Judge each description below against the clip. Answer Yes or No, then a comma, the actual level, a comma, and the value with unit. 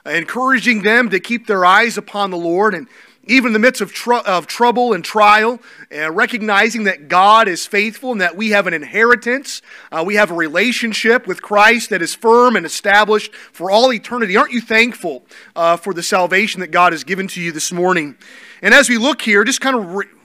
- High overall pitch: Yes, high, 215 Hz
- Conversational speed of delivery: No, fast, 210 wpm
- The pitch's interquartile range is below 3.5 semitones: No, average, 3.9 semitones